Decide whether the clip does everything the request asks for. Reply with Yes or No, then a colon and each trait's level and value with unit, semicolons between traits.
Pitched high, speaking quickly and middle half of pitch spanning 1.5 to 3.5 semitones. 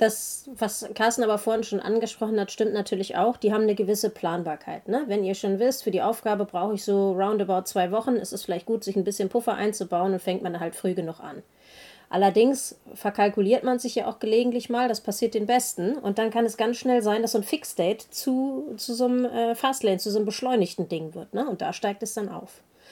Yes: high, 215 Hz; fast, 235 wpm; average, 2.8 semitones